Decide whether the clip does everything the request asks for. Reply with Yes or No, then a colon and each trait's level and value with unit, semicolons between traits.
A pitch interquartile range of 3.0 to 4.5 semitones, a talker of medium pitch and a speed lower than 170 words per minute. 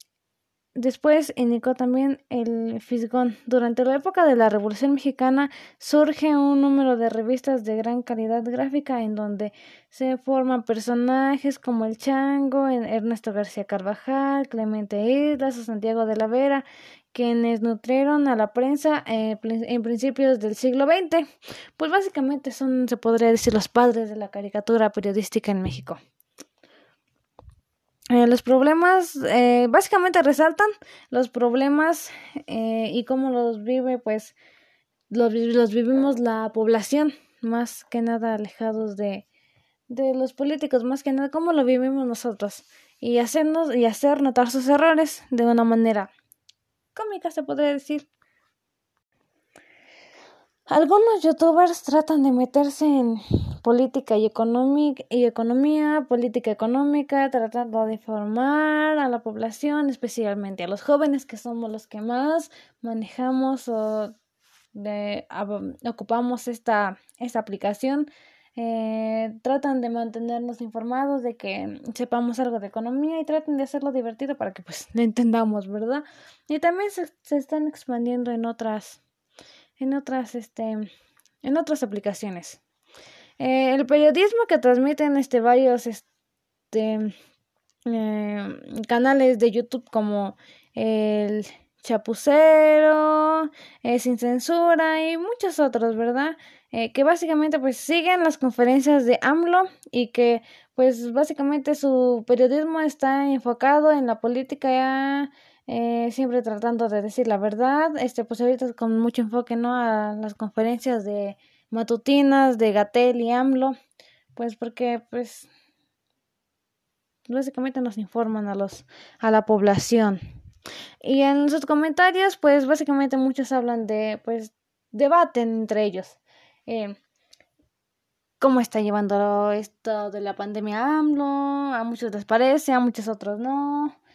No: average, 3.7 semitones; very high, 250 Hz; average, 130 wpm